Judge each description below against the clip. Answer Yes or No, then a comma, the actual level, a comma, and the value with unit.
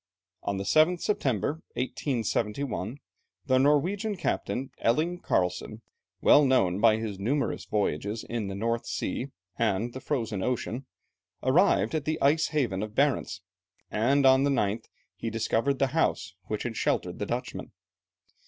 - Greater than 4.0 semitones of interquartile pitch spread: Yes, average, 4.8 semitones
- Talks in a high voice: No, low, 120 Hz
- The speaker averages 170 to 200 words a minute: No, average, 145 wpm